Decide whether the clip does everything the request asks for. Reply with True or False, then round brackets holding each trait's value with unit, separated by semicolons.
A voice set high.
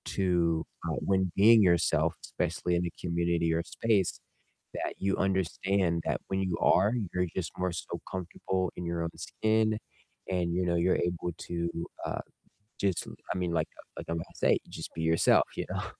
False (90 Hz)